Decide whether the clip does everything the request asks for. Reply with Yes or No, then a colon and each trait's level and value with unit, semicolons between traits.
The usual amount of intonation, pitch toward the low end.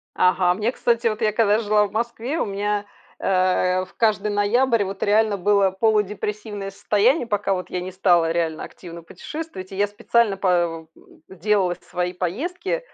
No: average, 3.1 semitones; high, 205 Hz